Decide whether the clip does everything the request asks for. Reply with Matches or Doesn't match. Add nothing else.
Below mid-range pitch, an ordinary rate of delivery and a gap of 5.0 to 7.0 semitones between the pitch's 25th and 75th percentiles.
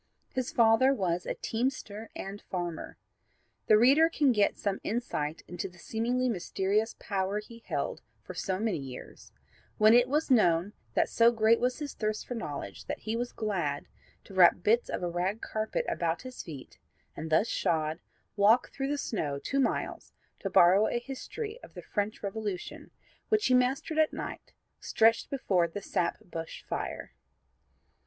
Doesn't match